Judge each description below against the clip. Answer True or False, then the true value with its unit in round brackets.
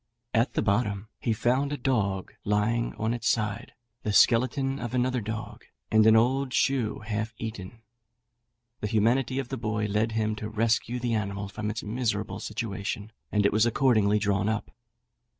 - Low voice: True (110 Hz)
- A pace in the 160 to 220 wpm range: True (170 wpm)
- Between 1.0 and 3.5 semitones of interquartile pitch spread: True (2.4 semitones)